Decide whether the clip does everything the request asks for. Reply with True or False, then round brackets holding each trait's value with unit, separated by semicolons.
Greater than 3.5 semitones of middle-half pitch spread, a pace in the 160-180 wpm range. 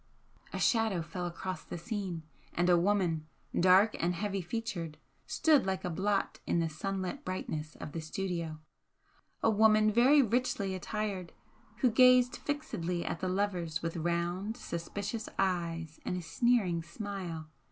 False (4.0 semitones; 145 wpm)